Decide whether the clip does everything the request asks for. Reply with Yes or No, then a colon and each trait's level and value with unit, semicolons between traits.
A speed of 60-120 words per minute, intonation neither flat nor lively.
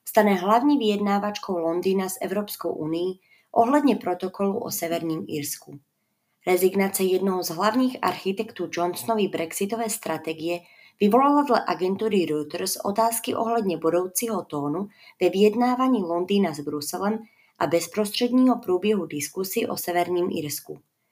Yes: slow, 115 wpm; average, 4.2 semitones